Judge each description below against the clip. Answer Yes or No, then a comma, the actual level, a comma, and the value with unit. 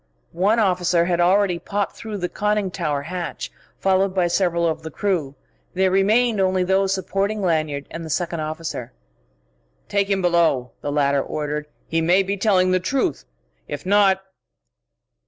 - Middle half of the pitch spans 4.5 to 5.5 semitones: No, average, 3.3 semitones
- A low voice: No, medium, 185 Hz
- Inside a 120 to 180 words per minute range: Yes, average, 155 wpm